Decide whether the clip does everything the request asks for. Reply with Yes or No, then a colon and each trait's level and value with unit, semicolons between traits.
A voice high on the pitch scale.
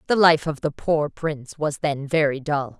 No: medium, 150 Hz